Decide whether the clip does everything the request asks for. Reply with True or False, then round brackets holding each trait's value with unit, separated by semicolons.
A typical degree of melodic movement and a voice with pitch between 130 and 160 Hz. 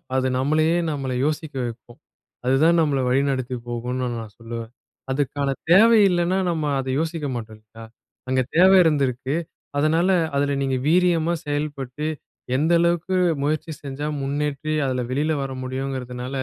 True (3.6 semitones; 140 Hz)